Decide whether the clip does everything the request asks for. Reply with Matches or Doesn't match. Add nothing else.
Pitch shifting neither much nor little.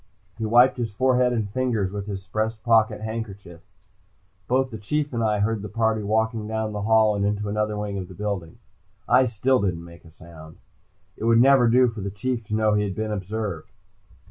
Doesn't match